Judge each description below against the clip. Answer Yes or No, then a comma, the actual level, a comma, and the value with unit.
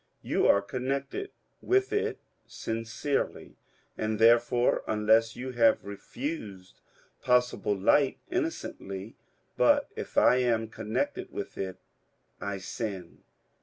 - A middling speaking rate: No, slow, 110 wpm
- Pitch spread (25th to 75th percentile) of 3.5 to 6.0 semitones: Yes, average, 3.9 semitones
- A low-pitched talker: Yes, low, 115 Hz